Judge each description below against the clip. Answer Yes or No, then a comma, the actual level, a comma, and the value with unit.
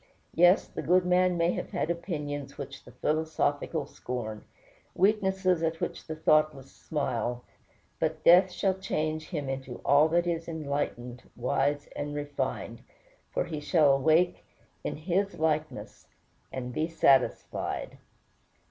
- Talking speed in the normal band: No, slow, 130 wpm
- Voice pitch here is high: No, medium, 155 Hz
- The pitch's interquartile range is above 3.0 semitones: Yes, average, 3.4 semitones